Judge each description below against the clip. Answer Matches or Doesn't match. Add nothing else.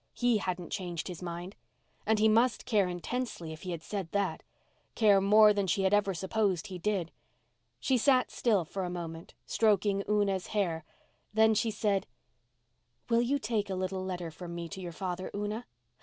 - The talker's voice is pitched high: Matches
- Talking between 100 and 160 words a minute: Doesn't match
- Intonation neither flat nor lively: Matches